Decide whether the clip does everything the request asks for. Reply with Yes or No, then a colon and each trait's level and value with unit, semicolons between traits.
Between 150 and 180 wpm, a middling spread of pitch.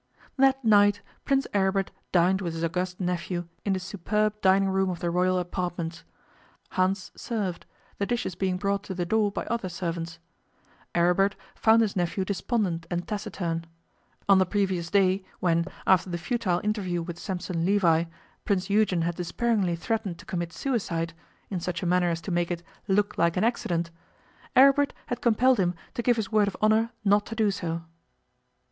Yes: average, 175 wpm; average, 3.1 semitones